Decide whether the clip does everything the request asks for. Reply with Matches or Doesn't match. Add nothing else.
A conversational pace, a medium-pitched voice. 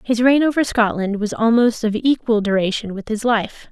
Doesn't match